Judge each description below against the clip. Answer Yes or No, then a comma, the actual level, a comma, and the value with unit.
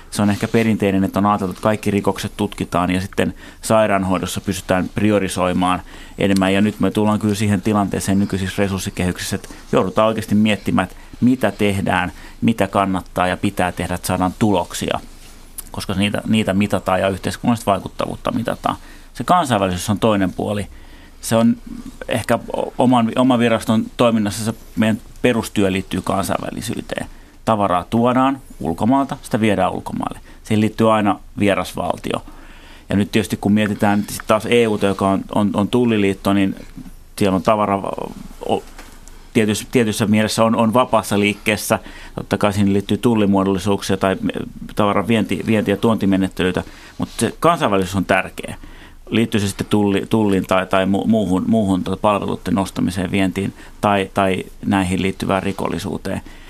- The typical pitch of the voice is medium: No, low, 100 Hz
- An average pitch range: No, narrow, 2.3 semitones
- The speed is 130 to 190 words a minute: Yes, average, 140 wpm